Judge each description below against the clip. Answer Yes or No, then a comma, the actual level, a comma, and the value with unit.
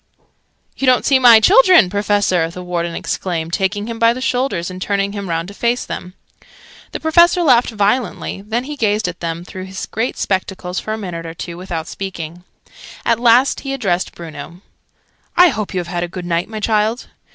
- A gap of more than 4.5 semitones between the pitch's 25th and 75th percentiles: Yes, average, 5.1 semitones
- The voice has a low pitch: No, high, 200 Hz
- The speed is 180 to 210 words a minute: Yes, average, 195 wpm